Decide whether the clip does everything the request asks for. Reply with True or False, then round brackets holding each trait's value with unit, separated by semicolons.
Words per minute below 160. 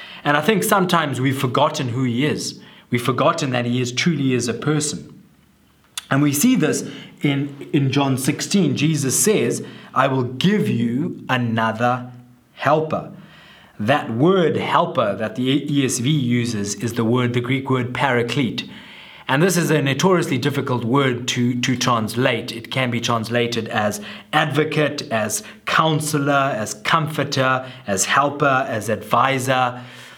True (145 wpm)